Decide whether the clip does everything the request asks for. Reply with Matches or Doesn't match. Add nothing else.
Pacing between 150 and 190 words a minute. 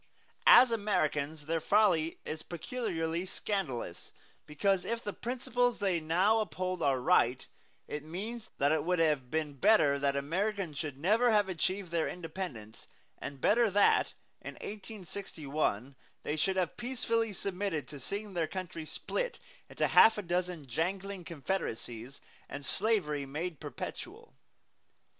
Doesn't match